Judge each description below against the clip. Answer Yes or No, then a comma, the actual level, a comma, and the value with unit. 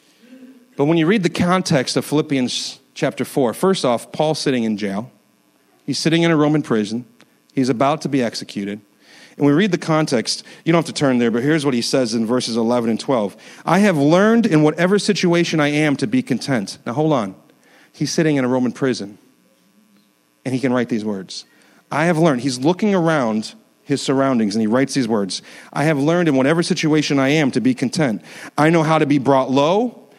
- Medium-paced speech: No, fast, 210 wpm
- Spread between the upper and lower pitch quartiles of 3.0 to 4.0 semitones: No, average, 4.8 semitones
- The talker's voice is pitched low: No, medium, 145 Hz